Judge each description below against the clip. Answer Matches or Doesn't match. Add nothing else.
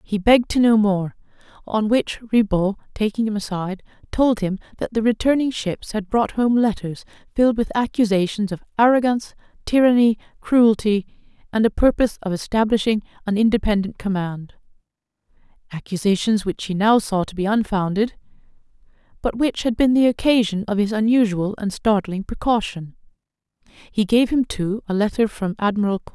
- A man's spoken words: Doesn't match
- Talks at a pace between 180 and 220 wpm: Doesn't match